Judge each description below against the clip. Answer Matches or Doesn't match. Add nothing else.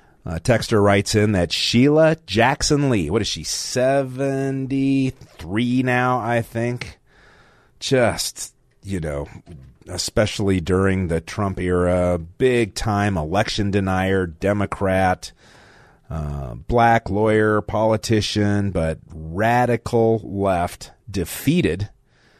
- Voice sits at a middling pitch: Doesn't match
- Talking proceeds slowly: Matches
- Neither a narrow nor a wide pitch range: Matches